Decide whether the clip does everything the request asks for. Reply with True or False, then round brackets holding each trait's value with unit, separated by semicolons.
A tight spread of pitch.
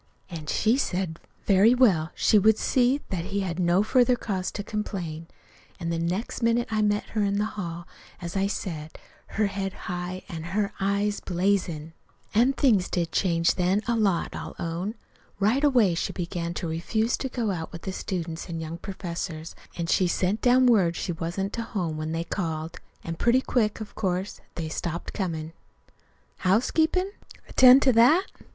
False (4.4 semitones)